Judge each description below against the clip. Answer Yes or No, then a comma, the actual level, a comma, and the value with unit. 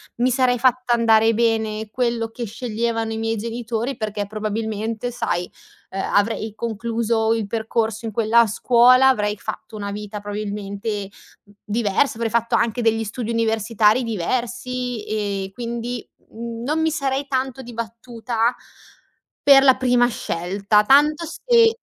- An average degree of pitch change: No, narrow, 2.3 semitones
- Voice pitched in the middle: No, high, 230 Hz